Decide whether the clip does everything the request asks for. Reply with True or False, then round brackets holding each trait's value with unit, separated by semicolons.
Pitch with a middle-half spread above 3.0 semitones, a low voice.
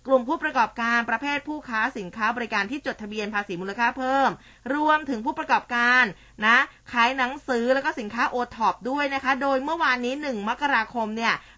False (3.6 semitones; 245 Hz)